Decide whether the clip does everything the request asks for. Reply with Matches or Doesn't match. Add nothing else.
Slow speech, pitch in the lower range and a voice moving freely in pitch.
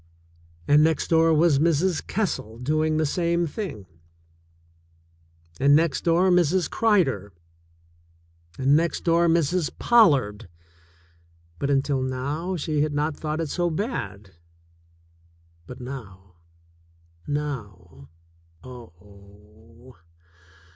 Doesn't match